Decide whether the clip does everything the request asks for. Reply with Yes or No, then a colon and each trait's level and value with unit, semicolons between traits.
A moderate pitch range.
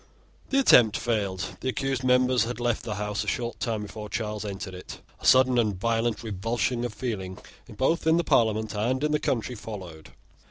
Yes: average, 3.4 semitones